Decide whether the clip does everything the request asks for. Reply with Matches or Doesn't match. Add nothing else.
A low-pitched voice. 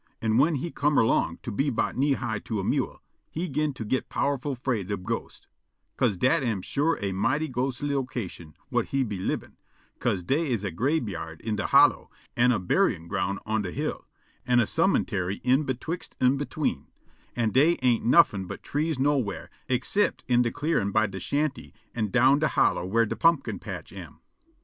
Matches